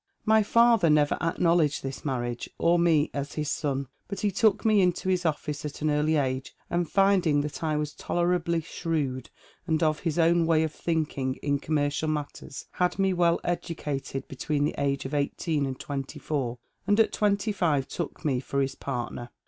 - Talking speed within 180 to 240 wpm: Yes, average, 190 wpm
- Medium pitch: Yes, medium, 155 Hz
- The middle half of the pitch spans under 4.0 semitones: Yes, average, 3.5 semitones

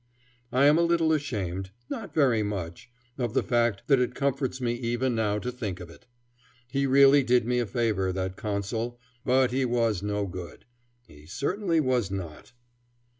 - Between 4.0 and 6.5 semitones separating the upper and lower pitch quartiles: Yes, average, 4.8 semitones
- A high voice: No, low, 120 Hz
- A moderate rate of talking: Yes, average, 175 wpm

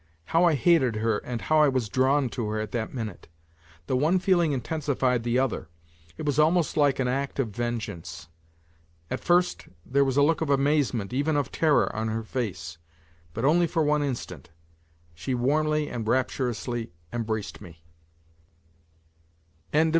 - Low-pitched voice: Yes, low, 130 Hz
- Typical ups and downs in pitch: Yes, average, 4.8 semitones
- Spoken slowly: No, average, 160 wpm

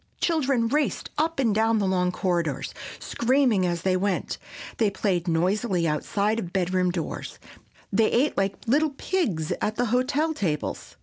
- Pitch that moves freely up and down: Yes, wide, 5.8 semitones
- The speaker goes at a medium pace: Yes, average, 150 wpm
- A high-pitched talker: Yes, high, 205 Hz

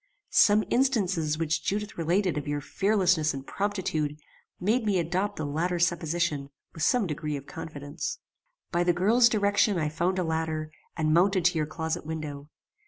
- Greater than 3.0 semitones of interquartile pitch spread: Yes, average, 4.2 semitones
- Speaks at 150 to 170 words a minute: Yes, average, 165 wpm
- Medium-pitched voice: Yes, medium, 170 Hz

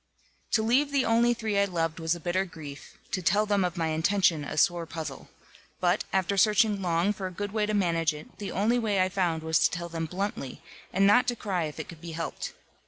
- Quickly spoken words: Yes, fast, 235 wpm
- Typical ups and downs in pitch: Yes, average, 3.9 semitones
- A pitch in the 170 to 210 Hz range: Yes, medium, 185 Hz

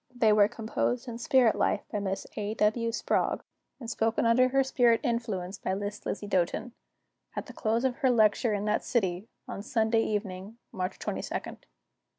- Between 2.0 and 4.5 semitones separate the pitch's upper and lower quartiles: Yes, narrow, 2.6 semitones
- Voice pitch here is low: No, high, 220 Hz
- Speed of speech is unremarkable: Yes, average, 165 wpm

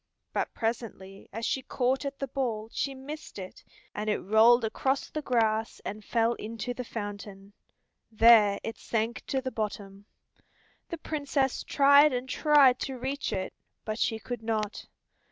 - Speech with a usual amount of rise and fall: Yes, average, 3.7 semitones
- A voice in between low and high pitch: No, high, 230 Hz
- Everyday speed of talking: Yes, average, 155 wpm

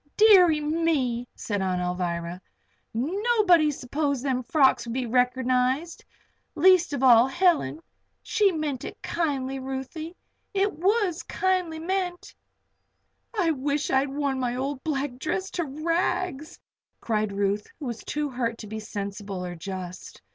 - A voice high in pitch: Yes, very high, 275 Hz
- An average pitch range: No, wide, 5.7 semitones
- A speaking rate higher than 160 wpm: No, slow, 135 wpm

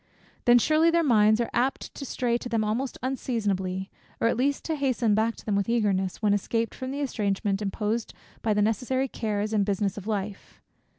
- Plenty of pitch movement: No, average, 3.5 semitones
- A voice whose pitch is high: Yes, high, 225 Hz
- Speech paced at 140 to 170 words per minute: No, average, 195 wpm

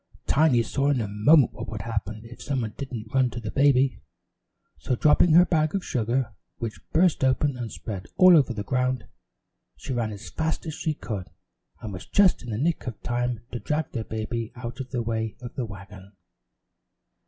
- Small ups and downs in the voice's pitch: No, average, 4.2 semitones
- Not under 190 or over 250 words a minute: Yes, average, 195 wpm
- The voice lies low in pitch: Yes, low, 120 Hz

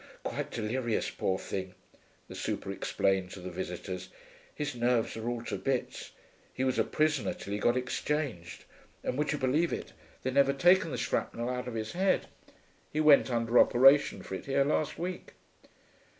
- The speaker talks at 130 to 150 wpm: No, average, 175 wpm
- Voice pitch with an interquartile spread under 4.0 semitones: No, average, 5.2 semitones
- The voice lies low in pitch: Yes, low, 125 Hz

